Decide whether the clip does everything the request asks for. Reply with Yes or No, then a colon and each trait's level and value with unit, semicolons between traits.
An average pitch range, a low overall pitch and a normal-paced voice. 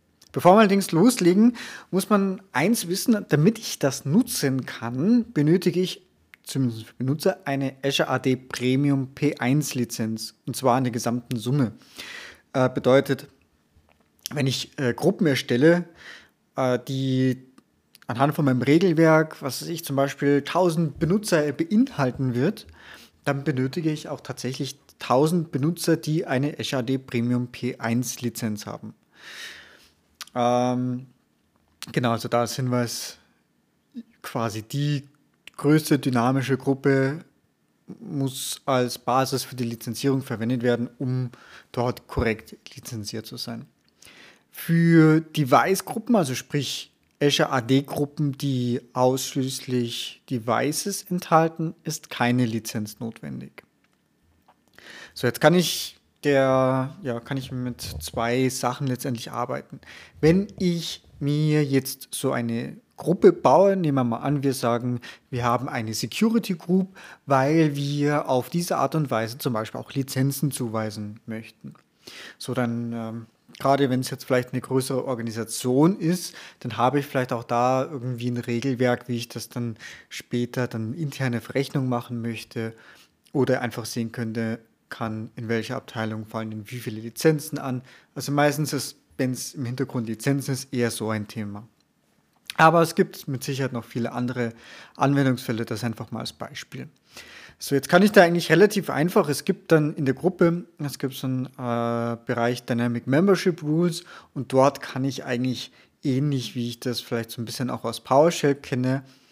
Yes: average, 3.8 semitones; low, 130 Hz; average, 140 wpm